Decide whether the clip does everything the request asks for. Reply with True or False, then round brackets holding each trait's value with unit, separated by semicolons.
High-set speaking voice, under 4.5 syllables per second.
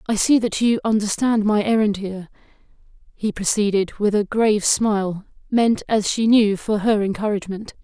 False (210 Hz; 5.1 syllables/s)